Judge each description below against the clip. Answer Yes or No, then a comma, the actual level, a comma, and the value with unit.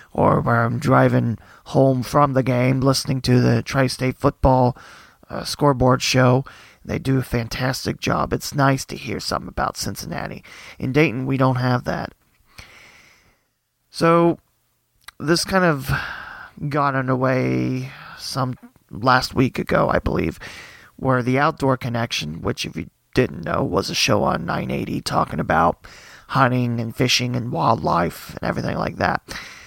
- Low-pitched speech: Yes, low, 130 Hz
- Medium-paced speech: Yes, average, 145 wpm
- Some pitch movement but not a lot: No, narrow, 1.8 semitones